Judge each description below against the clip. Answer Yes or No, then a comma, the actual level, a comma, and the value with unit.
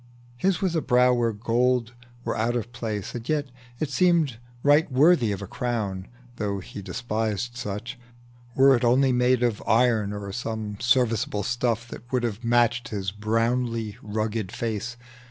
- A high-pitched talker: No, low, 120 Hz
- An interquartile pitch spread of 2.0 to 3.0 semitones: Yes, average, 2.7 semitones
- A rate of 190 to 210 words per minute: No, average, 160 wpm